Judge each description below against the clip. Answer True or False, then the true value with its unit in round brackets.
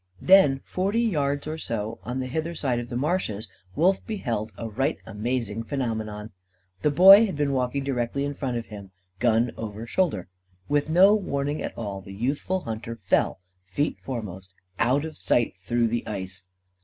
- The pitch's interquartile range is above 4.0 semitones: True (5.0 semitones)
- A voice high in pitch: False (125 Hz)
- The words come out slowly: False (170 wpm)